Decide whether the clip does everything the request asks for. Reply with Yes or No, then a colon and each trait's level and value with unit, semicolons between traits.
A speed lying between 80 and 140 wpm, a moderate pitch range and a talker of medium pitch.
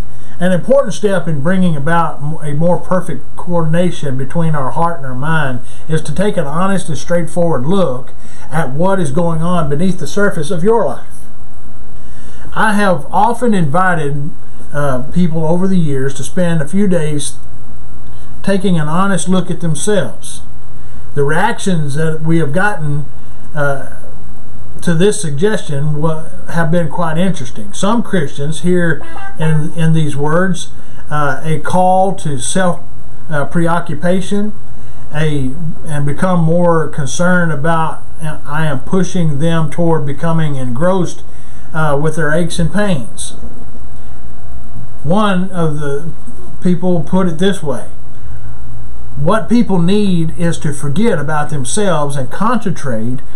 Yes: slow, 135 wpm; average, 4.0 semitones; medium, 165 Hz